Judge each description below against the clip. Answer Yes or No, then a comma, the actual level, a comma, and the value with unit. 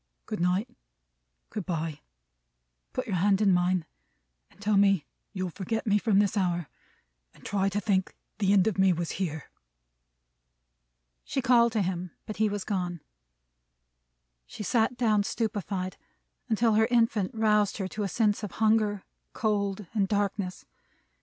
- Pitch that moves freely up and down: No, narrow, 2.6 semitones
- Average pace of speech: Yes, average, 150 wpm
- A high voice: Yes, high, 200 Hz